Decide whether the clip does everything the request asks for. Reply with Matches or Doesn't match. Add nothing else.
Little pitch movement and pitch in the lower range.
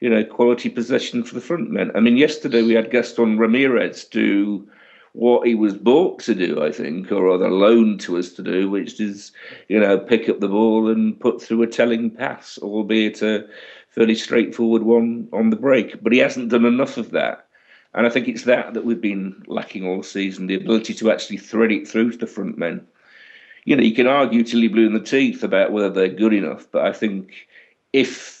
Matches